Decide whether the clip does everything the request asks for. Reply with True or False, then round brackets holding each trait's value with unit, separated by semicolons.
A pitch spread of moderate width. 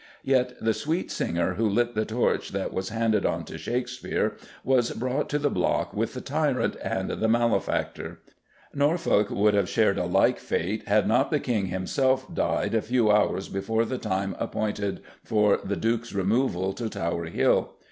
True (4.1 semitones)